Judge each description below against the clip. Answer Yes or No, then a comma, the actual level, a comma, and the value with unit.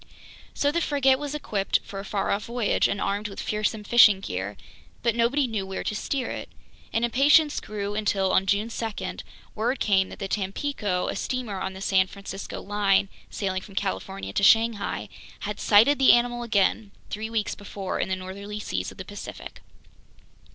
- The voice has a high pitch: Yes, high, 205 Hz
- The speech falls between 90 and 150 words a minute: No, average, 180 wpm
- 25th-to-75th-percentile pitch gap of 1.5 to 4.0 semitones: Yes, average, 3.3 semitones